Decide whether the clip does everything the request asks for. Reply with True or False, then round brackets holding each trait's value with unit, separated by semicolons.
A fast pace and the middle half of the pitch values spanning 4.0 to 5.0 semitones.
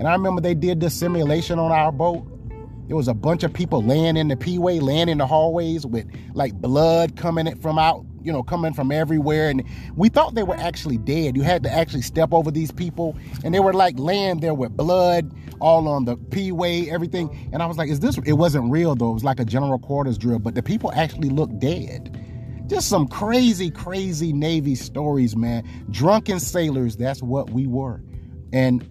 True (210 wpm; 4.7 semitones)